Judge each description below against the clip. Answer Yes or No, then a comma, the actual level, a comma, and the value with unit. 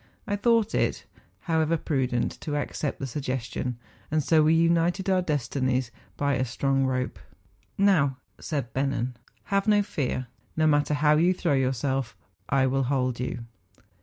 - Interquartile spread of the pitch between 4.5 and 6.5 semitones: No, average, 4.1 semitones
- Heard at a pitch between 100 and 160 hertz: Yes, medium, 140 Hz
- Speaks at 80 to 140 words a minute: No, average, 155 wpm